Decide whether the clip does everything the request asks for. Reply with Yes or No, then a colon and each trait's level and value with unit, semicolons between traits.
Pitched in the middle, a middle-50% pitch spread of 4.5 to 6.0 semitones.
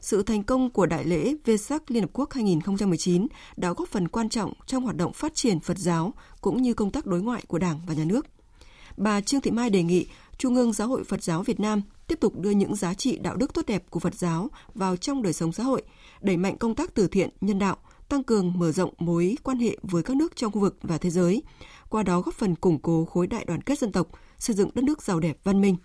No: high, 200 Hz; wide, 5.4 semitones